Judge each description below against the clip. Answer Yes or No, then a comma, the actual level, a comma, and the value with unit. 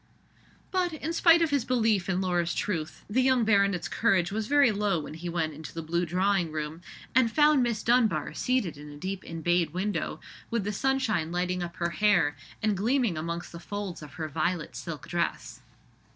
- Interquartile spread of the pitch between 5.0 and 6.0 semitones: Yes, average, 5.3 semitones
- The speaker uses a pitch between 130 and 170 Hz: No, medium, 185 Hz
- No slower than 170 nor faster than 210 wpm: Yes, average, 190 wpm